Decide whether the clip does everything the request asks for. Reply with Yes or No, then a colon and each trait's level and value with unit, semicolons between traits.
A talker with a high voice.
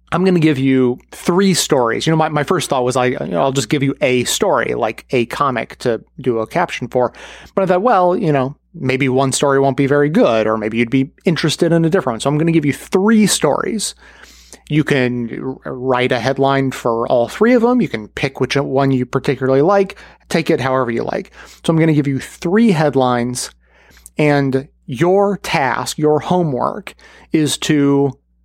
No: medium, 140 Hz